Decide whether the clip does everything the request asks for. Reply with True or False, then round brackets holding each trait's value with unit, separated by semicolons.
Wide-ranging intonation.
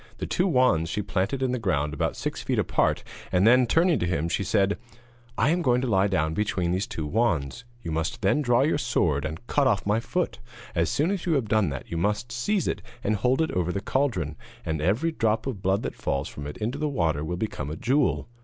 True (7.3 semitones)